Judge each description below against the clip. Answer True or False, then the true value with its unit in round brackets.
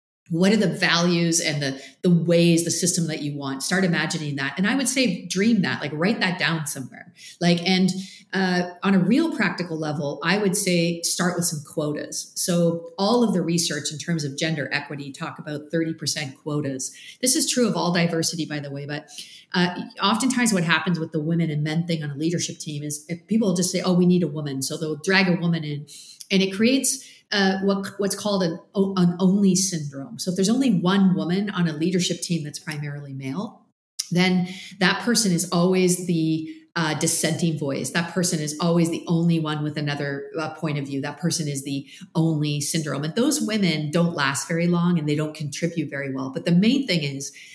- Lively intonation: False (3.4 semitones)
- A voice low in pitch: False (170 Hz)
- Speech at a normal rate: False (210 wpm)